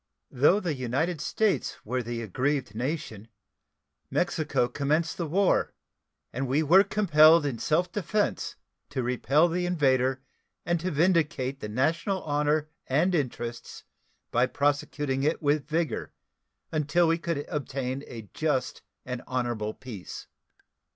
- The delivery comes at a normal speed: No, slow, 130 wpm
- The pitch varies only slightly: No, average, 4.5 semitones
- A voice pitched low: No, medium, 145 Hz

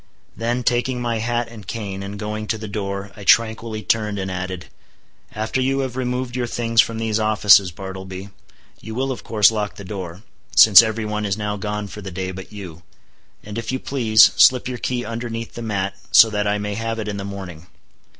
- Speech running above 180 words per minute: Yes, average, 200 wpm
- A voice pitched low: Yes, low, 110 Hz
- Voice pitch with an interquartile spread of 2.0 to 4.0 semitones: Yes, narrow, 2.6 semitones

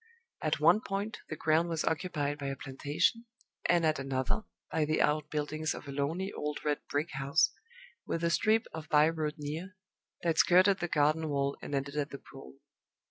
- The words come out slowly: No, average, 190 wpm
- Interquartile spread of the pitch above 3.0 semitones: No, average, 2.7 semitones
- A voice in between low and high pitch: Yes, medium, 155 Hz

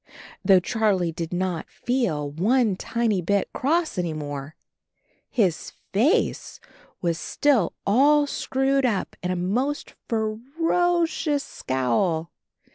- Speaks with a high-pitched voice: Yes, high, 205 Hz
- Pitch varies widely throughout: Yes, wide, 7.8 semitones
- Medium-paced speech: No, slow, 120 wpm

